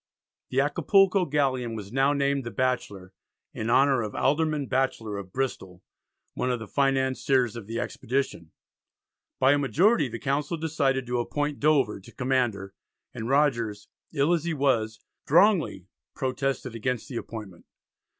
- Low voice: Yes, low, 130 Hz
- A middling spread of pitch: Yes, average, 3.9 semitones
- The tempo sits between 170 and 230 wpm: No, average, 150 wpm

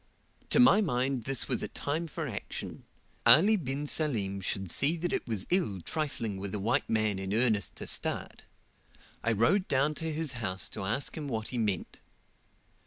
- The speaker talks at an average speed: Yes, average, 185 wpm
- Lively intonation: Yes, wide, 6.8 semitones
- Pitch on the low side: Yes, low, 125 Hz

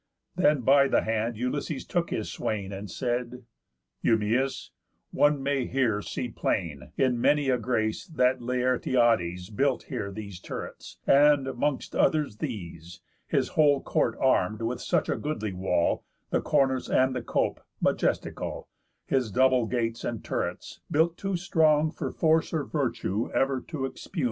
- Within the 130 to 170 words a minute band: Yes, average, 145 wpm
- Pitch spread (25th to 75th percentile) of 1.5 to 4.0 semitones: No, average, 4.6 semitones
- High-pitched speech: No, low, 125 Hz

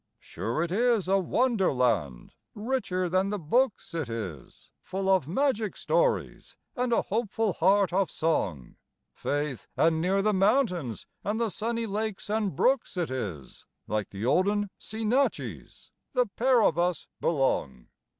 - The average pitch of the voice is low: No, high, 190 Hz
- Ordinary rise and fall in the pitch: No, wide, 6.7 semitones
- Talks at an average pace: Yes, average, 145 wpm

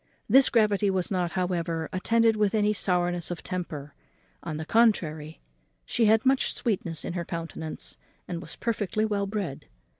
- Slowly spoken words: No, average, 155 wpm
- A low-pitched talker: No, medium, 185 Hz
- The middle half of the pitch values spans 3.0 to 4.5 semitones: Yes, average, 4.2 semitones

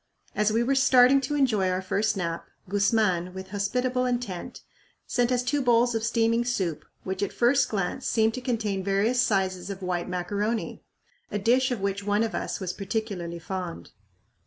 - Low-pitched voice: No, high, 210 Hz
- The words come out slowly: No, average, 175 wpm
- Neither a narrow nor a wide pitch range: Yes, average, 4.3 semitones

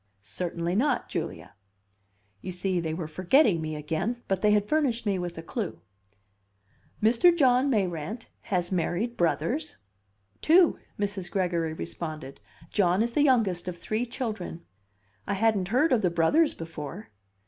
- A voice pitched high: Yes, high, 195 Hz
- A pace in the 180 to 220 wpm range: No, average, 145 wpm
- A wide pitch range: Yes, wide, 5.7 semitones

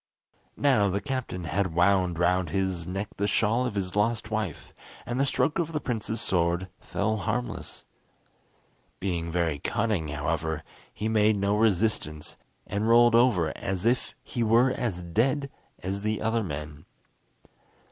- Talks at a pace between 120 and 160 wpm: Yes, average, 145 wpm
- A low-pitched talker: Yes, low, 100 Hz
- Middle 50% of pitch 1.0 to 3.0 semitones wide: No, average, 4.6 semitones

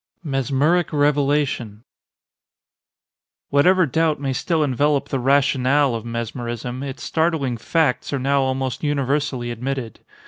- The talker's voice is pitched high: No, low, 135 Hz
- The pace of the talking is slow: Yes, slow, 110 wpm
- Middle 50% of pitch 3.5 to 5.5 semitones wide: No, narrow, 2.6 semitones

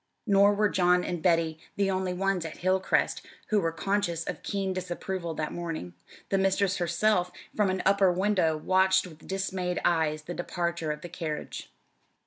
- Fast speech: No, average, 165 wpm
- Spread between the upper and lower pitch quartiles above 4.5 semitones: No, narrow, 2.5 semitones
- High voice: No, medium, 180 Hz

